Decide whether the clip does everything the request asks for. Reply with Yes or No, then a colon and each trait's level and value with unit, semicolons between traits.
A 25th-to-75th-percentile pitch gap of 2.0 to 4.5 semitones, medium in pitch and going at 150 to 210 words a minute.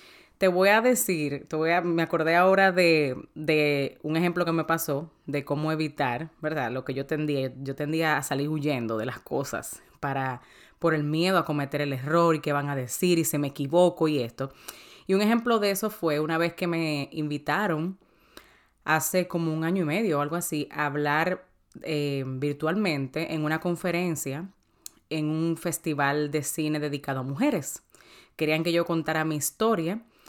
Yes: average, 2.9 semitones; medium, 155 Hz; average, 185 wpm